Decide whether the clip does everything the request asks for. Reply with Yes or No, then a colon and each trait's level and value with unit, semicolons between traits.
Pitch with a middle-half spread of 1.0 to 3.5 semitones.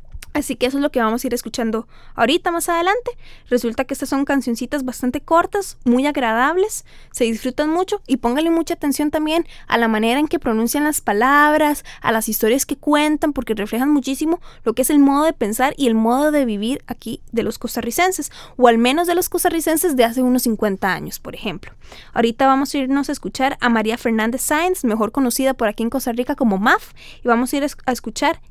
No: average, 4.1 semitones